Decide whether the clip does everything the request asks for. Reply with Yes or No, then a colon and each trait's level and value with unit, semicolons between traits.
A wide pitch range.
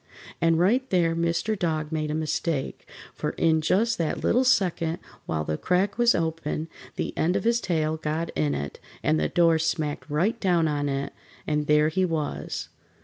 No: average, 3.0 semitones